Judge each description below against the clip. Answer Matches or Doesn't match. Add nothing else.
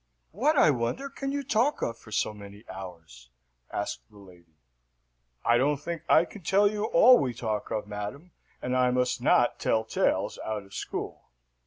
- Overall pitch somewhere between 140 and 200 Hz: Doesn't match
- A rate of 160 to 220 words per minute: Matches